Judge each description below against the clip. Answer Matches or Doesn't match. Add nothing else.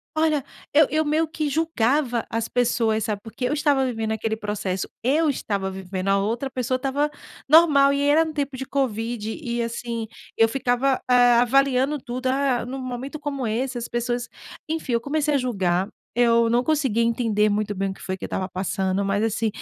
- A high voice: Matches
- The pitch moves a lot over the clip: Doesn't match